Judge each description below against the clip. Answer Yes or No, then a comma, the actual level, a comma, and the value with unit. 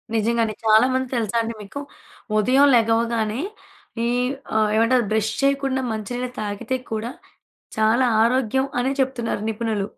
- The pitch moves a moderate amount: Yes, average, 3.0 semitones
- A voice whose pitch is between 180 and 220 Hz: No, high, 230 Hz